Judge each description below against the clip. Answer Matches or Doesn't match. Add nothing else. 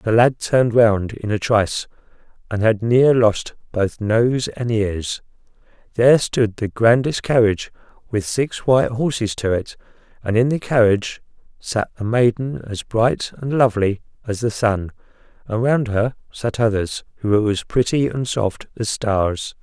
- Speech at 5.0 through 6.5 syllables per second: Doesn't match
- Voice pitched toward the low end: Matches